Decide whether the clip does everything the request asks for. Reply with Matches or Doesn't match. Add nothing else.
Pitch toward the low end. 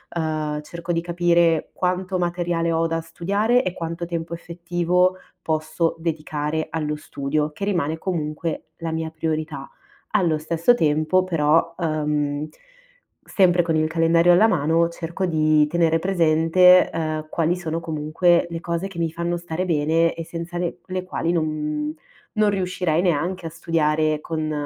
Doesn't match